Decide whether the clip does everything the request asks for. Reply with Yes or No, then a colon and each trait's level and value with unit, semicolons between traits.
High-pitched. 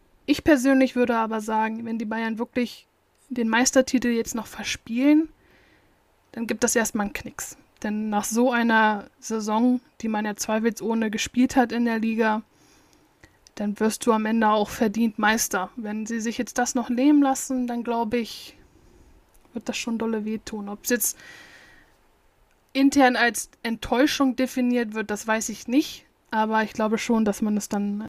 Yes: high, 230 Hz